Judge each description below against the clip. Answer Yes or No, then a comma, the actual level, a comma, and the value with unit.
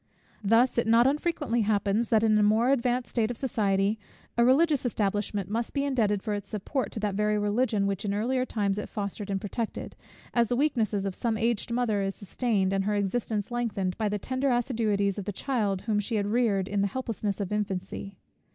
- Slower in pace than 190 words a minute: No, fast, 205 wpm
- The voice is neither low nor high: No, high, 215 Hz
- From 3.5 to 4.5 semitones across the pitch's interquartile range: No, average, 3.1 semitones